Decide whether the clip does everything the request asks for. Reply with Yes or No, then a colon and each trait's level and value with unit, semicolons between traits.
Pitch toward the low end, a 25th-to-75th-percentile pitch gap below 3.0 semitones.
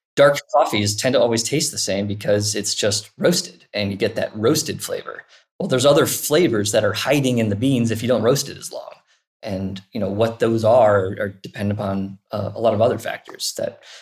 Yes: low, 105 Hz; narrow, 2.5 semitones